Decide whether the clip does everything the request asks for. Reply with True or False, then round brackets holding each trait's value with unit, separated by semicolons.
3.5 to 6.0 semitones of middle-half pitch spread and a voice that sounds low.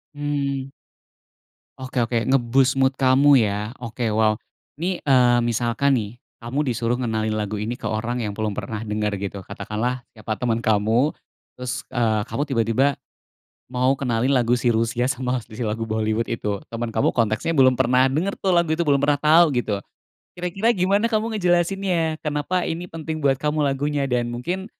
True (4.4 semitones; 125 Hz)